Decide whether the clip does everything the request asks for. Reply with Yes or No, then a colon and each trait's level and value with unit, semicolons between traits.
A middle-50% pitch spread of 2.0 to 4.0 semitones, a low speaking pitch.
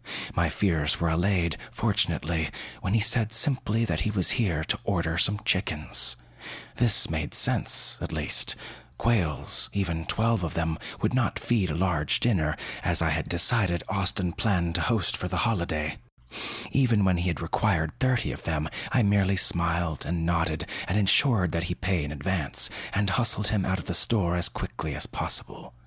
No: average, 4.5 semitones; very low, 95 Hz